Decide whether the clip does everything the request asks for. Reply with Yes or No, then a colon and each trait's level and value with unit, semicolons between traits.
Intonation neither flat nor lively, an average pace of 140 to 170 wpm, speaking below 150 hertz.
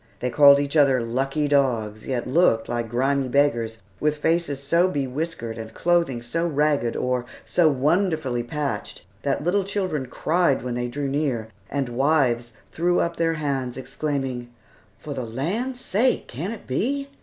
Yes: average, 4.8 semitones; average, 155 wpm; medium, 140 Hz